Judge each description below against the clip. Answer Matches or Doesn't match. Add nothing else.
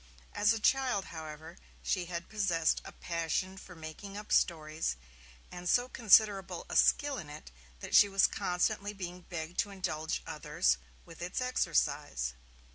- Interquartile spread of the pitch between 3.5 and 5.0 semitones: Matches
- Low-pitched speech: Doesn't match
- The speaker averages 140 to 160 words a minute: Matches